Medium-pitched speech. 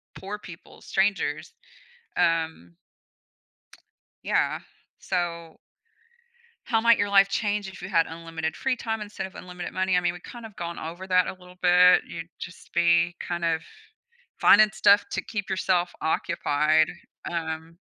Yes: medium, 180 Hz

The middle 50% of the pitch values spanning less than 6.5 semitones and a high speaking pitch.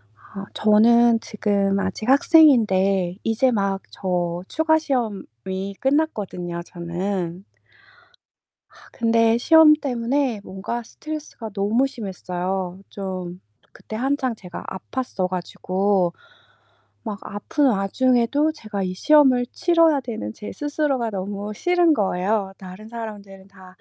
Yes: average, 5.3 semitones; high, 210 Hz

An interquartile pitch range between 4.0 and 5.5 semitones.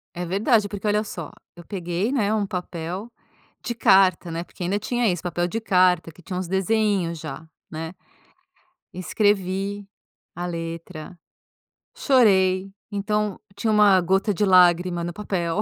No: average, 3.0 semitones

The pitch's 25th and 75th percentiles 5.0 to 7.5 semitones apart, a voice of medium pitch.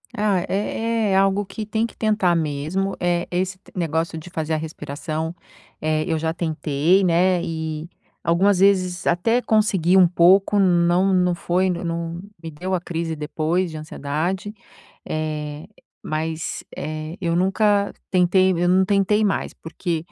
No: average, 3.0 semitones; medium, 175 Hz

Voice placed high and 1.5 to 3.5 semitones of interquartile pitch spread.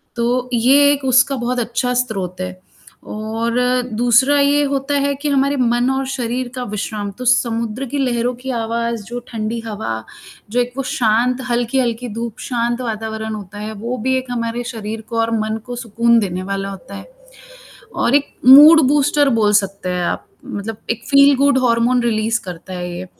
Yes: high, 235 Hz; average, 2.8 semitones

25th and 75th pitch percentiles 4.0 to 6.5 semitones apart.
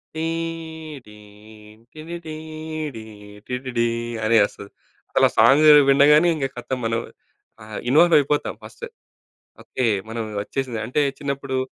Yes: average, 4.4 semitones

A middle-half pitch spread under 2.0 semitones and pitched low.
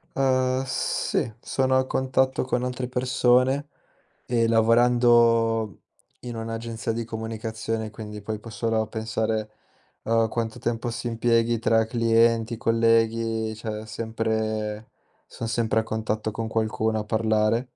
Yes: narrow, 1.3 semitones; low, 115 Hz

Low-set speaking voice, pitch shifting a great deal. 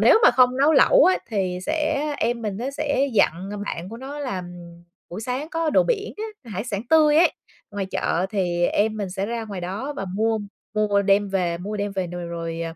No: high, 215 Hz; wide, 6.5 semitones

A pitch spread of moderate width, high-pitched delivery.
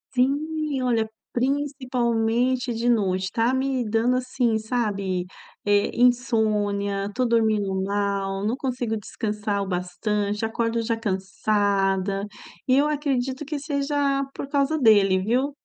Yes: average, 4.2 semitones; high, 230 Hz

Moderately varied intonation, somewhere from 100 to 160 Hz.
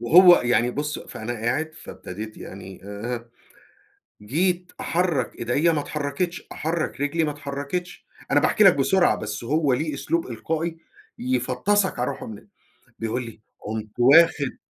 No: wide, 5.8 semitones; medium, 140 Hz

